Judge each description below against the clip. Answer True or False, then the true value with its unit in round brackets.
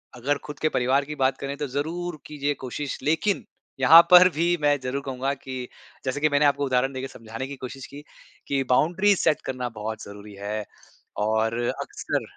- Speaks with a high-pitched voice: False (140 Hz)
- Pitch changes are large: False (2.9 semitones)